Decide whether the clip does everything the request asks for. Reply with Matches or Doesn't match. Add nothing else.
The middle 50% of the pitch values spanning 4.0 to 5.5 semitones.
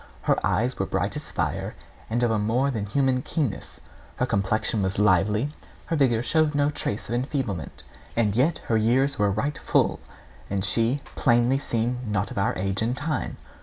Matches